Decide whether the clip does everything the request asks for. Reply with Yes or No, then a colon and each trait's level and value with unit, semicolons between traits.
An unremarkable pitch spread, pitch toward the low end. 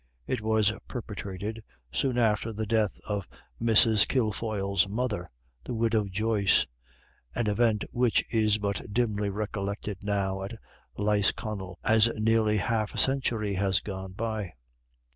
No: narrow, 2.1 semitones; low, 105 Hz